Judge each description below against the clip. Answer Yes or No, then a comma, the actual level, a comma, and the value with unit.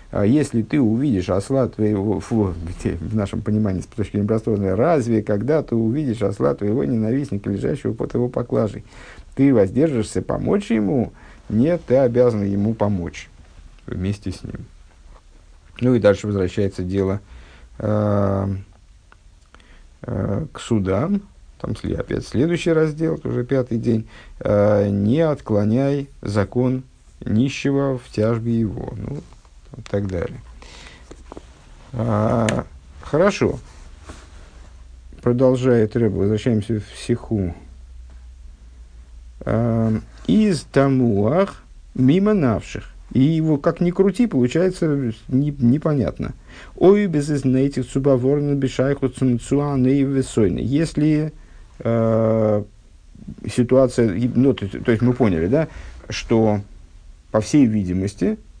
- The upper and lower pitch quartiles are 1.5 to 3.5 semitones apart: No, wide, 5.5 semitones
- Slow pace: Yes, slow, 105 wpm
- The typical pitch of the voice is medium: No, low, 110 Hz